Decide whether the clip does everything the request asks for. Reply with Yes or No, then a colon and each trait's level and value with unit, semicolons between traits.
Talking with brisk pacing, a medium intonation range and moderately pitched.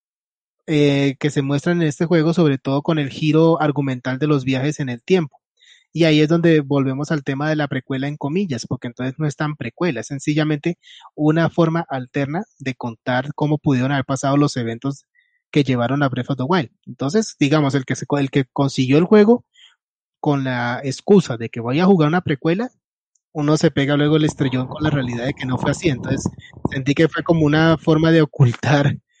Yes: fast, 205 wpm; average, 3.1 semitones; medium, 150 Hz